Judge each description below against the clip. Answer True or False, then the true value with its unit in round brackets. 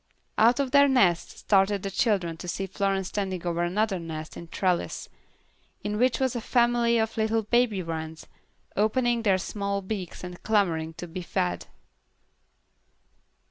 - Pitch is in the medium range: False (200 Hz)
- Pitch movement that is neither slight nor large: True (4.3 semitones)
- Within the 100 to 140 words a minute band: False (155 wpm)